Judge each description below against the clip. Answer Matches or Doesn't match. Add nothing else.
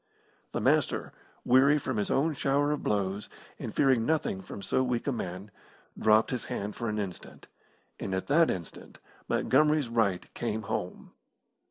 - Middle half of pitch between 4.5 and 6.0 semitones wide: Matches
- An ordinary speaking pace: Matches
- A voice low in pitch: Matches